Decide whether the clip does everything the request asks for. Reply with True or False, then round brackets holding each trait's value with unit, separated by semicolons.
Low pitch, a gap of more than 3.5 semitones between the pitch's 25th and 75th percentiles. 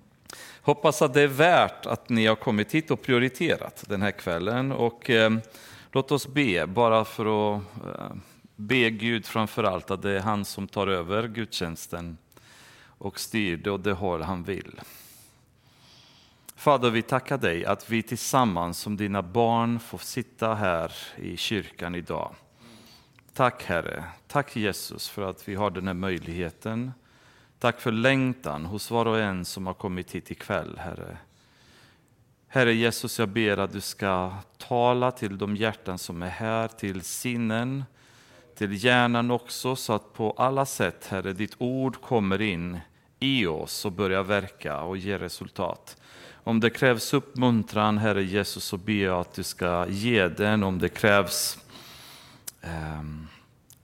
True (110 Hz; 4.1 semitones)